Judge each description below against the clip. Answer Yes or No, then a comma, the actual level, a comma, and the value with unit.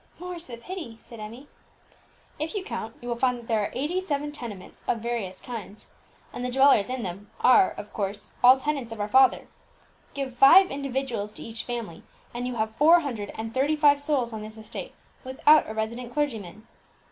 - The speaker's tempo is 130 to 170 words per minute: No, average, 195 wpm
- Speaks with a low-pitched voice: No, high, 245 Hz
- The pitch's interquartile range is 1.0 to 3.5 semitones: No, average, 4.3 semitones